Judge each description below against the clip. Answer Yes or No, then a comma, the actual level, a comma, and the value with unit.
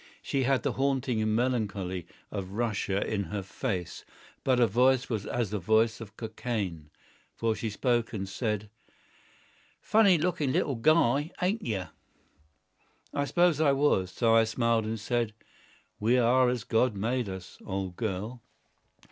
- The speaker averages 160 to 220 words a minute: No, average, 145 wpm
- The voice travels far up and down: No, average, 3.9 semitones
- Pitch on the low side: Yes, low, 115 Hz